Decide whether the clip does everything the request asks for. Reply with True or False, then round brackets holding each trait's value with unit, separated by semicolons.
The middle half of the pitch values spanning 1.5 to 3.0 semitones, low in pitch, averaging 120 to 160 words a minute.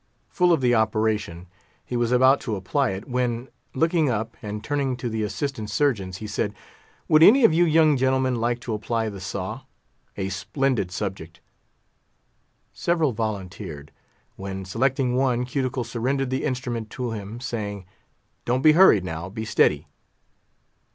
False (4.3 semitones; 120 Hz; 150 wpm)